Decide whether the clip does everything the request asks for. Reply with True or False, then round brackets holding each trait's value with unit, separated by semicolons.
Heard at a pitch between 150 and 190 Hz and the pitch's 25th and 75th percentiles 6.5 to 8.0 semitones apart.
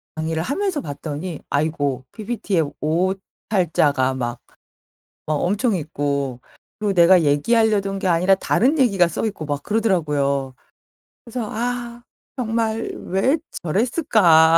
True (185 Hz; 6.8 semitones)